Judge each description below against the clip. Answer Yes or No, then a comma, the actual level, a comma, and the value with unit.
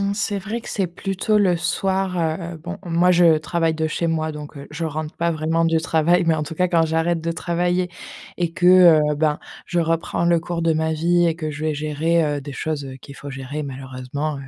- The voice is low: No, medium, 165 Hz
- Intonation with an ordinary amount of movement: No, narrow, 2.2 semitones